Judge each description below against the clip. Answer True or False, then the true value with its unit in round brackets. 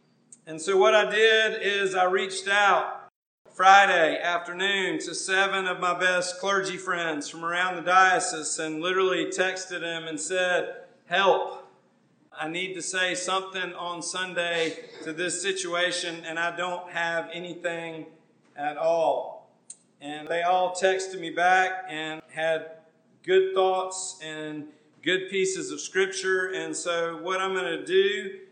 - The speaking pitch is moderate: True (180 Hz)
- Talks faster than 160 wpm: False (145 wpm)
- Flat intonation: True (2.2 semitones)